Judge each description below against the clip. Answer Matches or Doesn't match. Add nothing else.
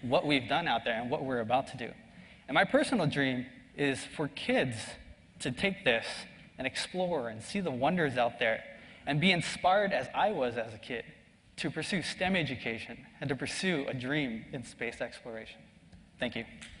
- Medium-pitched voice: Matches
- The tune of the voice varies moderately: Doesn't match